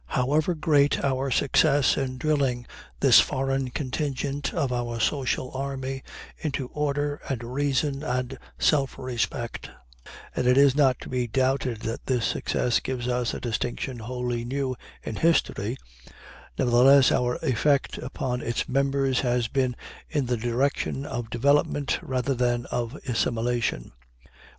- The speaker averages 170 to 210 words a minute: No, slow, 135 wpm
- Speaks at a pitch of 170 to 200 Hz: No, low, 130 Hz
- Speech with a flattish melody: Yes, narrow, 2.3 semitones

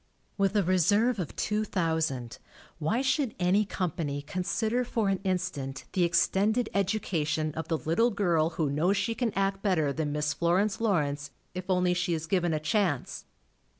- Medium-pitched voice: Yes, medium, 180 Hz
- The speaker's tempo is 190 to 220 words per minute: No, average, 170 wpm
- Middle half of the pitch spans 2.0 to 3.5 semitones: No, average, 4.6 semitones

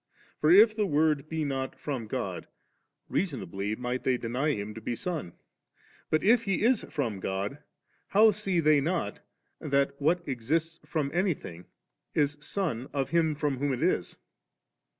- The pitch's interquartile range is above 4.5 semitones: Yes, average, 5.1 semitones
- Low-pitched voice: No, medium, 145 Hz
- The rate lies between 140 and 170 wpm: Yes, average, 155 wpm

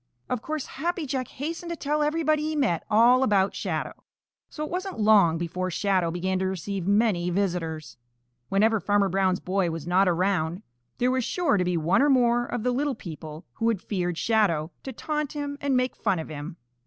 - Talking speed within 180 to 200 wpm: Yes, average, 195 wpm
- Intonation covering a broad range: Yes, wide, 7.0 semitones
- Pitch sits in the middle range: No, high, 205 Hz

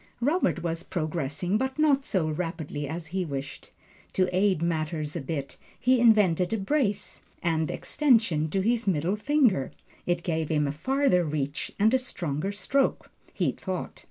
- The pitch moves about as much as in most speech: No, wide, 6.2 semitones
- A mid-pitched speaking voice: Yes, medium, 180 Hz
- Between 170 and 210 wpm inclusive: No, average, 155 wpm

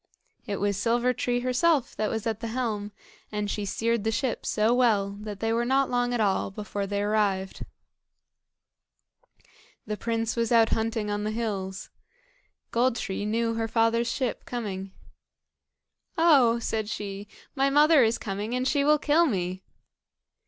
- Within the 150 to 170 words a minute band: Yes, average, 160 wpm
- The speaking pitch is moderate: No, high, 225 Hz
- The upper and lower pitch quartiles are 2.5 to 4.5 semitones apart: Yes, average, 2.9 semitones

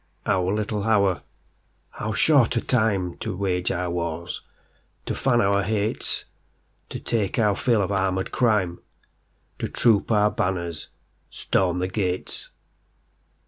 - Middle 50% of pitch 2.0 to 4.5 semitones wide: Yes, average, 3.0 semitones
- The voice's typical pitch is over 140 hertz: No, low, 100 Hz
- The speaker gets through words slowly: Yes, slow, 110 wpm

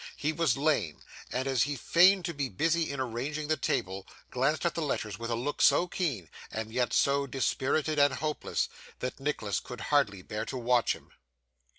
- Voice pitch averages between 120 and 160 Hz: Yes, low, 135 Hz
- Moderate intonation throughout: Yes, average, 4.5 semitones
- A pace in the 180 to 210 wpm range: Yes, average, 190 wpm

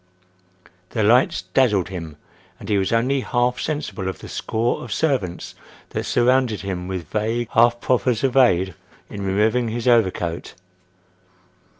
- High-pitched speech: No, low, 110 Hz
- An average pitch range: Yes, average, 4.5 semitones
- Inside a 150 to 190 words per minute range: No, average, 140 wpm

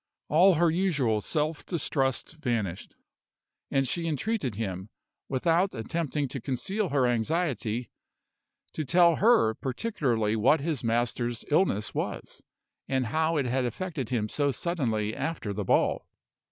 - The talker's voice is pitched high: No, low, 135 Hz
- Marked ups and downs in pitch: Yes, wide, 6.3 semitones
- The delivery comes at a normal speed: No, slow, 130 wpm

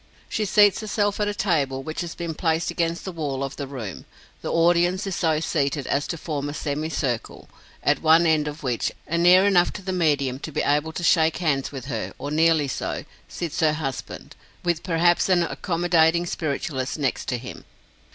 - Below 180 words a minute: No, average, 195 wpm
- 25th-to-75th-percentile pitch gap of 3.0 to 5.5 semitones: Yes, average, 3.4 semitones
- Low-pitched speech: No, medium, 160 Hz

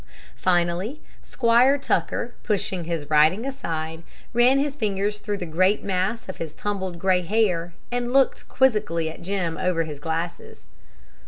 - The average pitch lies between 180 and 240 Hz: Yes, high, 190 Hz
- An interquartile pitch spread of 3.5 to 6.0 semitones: Yes, wide, 5.5 semitones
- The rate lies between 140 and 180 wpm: Yes, average, 145 wpm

